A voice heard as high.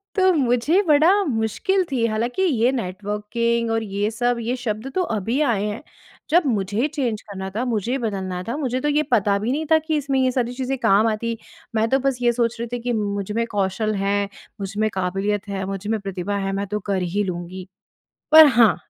Yes: high, 225 Hz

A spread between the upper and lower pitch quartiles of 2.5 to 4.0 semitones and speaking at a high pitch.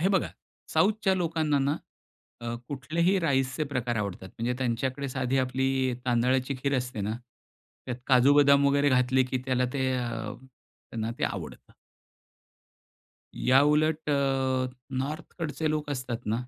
No: average, 2.8 semitones; low, 135 Hz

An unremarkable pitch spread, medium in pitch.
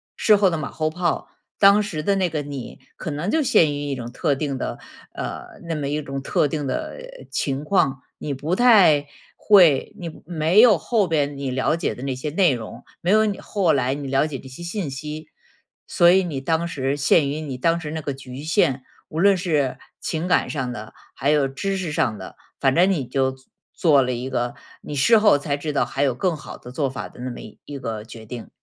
Yes: average, 4.3 semitones; medium, 150 Hz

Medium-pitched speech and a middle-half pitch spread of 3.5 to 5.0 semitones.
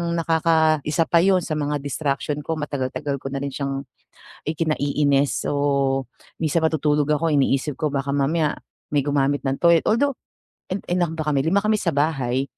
No: medium, 150 Hz; average, 2.7 semitones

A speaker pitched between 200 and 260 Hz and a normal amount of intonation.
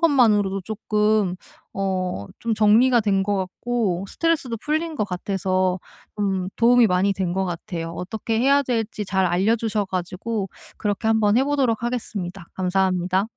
Yes: high, 205 Hz; average, 3.6 semitones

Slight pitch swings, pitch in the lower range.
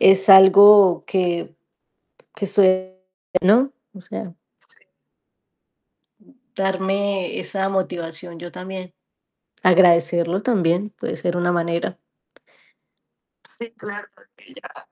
No: narrow, 2.2 semitones; medium, 185 Hz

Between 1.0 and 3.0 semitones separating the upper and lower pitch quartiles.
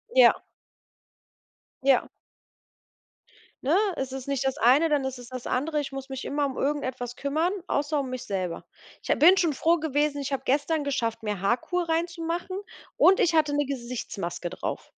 No: average, 3.6 semitones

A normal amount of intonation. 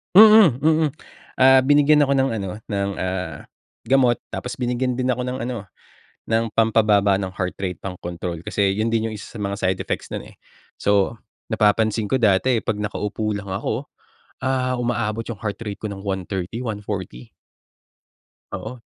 Yes: average, 4.1 semitones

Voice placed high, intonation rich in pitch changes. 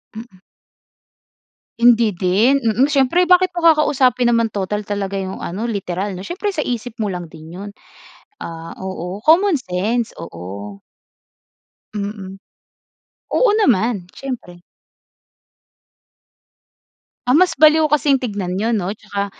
Yes: high, 215 Hz; wide, 6.0 semitones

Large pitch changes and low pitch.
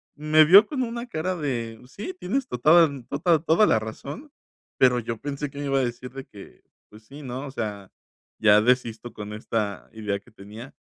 Yes: wide, 5.9 semitones; low, 130 Hz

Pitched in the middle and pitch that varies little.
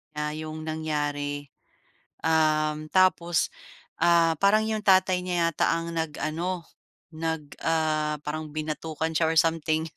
Yes: medium, 160 Hz; narrow, 1.5 semitones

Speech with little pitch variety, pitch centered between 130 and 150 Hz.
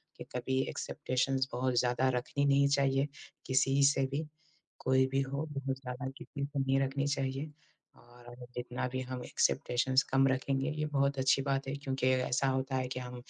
Yes: narrow, 1.2 semitones; low, 135 Hz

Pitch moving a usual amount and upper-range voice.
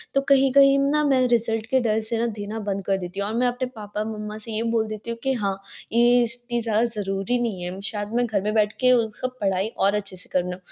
Yes: average, 3.0 semitones; high, 220 Hz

